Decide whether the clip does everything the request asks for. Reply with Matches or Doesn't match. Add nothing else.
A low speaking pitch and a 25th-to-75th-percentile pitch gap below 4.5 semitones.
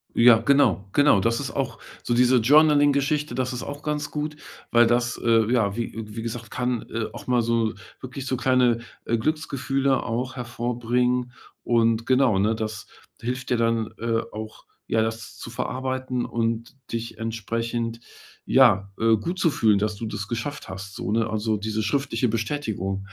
Matches